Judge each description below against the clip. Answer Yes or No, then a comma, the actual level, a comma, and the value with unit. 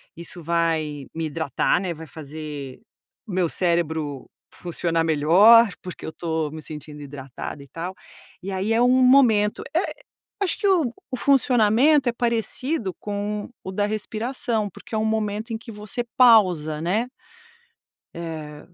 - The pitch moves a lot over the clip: Yes, wide, 6.1 semitones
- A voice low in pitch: No, high, 190 Hz